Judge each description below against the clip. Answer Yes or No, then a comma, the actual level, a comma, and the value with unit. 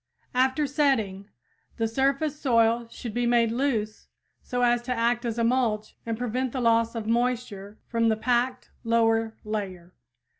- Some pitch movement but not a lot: No, narrow, 1.9 semitones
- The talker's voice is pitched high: Yes, high, 235 Hz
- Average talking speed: Yes, average, 155 wpm